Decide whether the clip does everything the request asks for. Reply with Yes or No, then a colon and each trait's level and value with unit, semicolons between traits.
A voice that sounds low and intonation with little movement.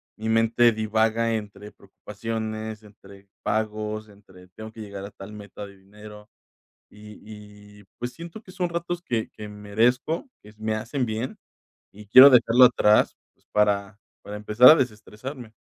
Yes: low, 110 Hz; narrow, 1.8 semitones